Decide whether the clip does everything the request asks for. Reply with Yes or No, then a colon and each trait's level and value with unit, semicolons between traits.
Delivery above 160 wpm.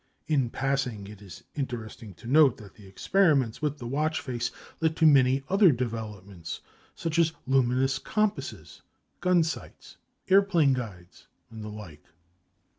No: average, 140 wpm